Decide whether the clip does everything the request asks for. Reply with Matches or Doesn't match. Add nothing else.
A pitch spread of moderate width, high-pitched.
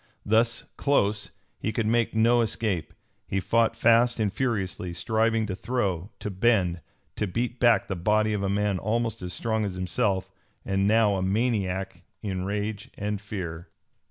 Doesn't match